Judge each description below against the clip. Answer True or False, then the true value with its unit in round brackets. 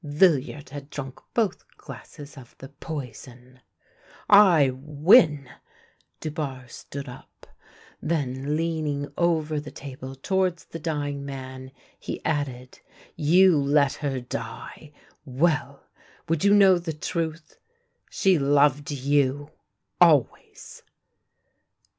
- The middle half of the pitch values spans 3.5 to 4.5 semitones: False (3.1 semitones)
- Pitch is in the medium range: True (145 Hz)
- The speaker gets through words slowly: True (115 wpm)